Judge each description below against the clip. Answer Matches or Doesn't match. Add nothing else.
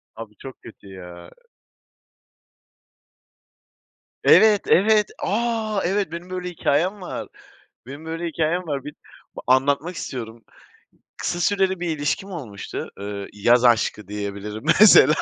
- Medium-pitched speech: Matches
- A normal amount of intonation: Doesn't match